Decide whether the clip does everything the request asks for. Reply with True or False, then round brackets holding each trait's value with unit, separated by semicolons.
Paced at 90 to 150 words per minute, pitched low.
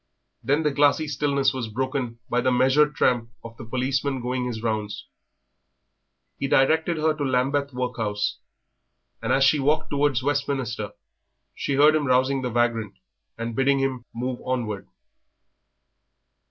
True (140 wpm; 130 Hz)